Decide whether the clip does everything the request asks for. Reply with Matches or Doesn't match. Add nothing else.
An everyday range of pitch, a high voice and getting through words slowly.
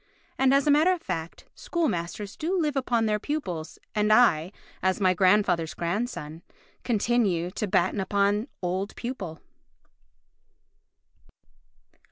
Doesn't match